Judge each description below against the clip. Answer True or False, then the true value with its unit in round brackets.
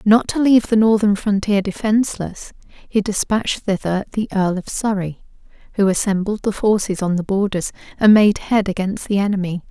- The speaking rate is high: False (165 wpm)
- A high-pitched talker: True (200 Hz)